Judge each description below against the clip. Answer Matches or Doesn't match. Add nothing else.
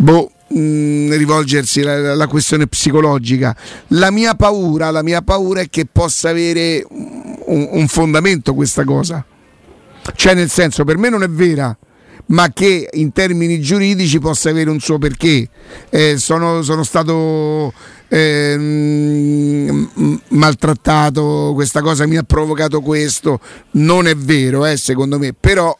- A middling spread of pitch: Doesn't match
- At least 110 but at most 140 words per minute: Matches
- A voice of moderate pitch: Matches